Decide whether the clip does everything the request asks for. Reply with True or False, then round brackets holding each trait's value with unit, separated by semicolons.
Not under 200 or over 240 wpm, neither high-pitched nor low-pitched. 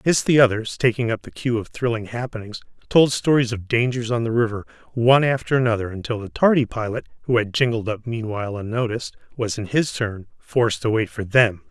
False (205 wpm; 115 Hz)